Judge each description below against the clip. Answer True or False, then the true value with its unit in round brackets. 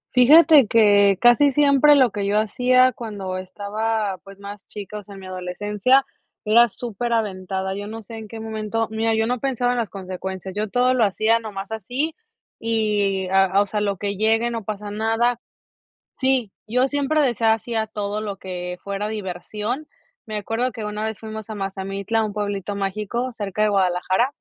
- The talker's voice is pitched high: True (215 Hz)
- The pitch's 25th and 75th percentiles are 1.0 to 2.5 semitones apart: False (2.9 semitones)